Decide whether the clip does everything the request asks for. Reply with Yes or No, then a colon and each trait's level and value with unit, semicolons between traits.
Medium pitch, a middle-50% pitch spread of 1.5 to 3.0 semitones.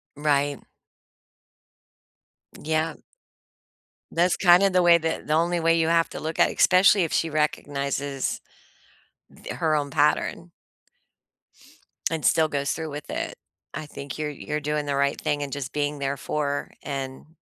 Yes: medium, 150 Hz; narrow, 2.4 semitones